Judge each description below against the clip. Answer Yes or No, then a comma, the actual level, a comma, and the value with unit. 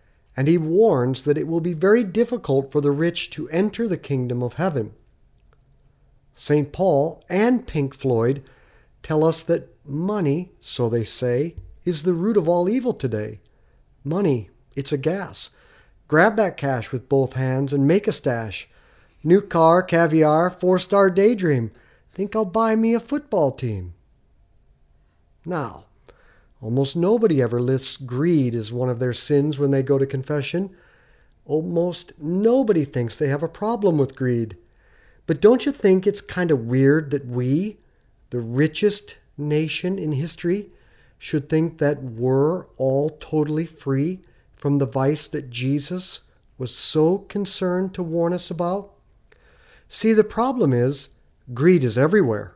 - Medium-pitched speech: Yes, medium, 150 Hz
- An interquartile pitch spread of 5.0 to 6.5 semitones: Yes, wide, 5.5 semitones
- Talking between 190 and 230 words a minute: No, average, 150 wpm